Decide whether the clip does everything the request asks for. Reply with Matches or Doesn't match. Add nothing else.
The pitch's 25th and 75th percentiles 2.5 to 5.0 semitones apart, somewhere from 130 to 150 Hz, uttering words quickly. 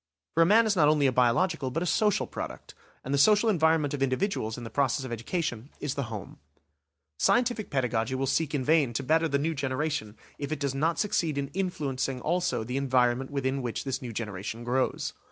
Matches